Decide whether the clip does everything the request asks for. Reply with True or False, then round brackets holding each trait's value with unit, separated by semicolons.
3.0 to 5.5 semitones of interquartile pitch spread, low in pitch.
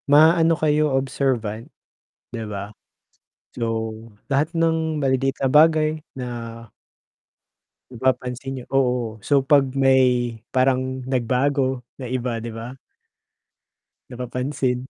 False (2.6 semitones; 130 Hz)